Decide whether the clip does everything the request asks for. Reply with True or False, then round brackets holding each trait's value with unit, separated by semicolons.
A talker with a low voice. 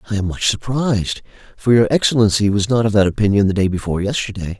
True (105 Hz)